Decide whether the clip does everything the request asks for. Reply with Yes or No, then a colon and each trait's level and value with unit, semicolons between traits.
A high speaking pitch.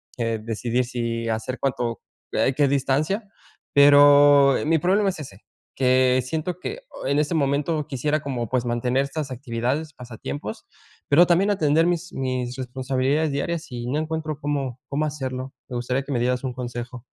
No: low, 135 Hz